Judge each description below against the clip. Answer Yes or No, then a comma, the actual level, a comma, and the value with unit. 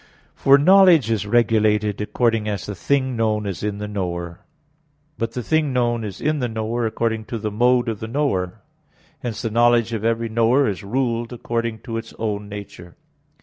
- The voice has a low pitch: Yes, low, 115 Hz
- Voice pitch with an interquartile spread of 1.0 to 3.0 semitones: Yes, narrow, 2.4 semitones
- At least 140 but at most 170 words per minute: No, average, 185 wpm